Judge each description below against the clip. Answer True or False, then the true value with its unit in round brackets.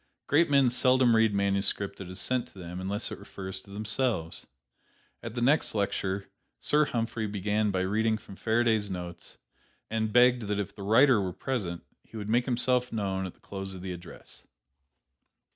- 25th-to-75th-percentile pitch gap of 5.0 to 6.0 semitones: False (3.8 semitones)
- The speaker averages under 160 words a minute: False (175 wpm)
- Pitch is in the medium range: False (105 Hz)